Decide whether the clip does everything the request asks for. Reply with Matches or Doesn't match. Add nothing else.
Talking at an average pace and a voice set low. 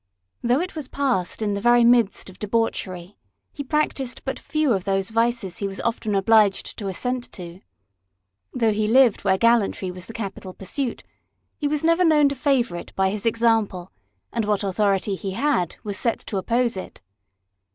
Doesn't match